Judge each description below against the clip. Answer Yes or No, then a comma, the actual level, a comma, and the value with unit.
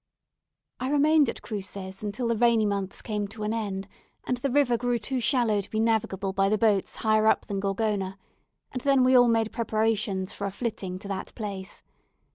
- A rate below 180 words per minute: No, average, 195 wpm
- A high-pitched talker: Yes, high, 215 Hz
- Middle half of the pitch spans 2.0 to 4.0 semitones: Yes, average, 3.2 semitones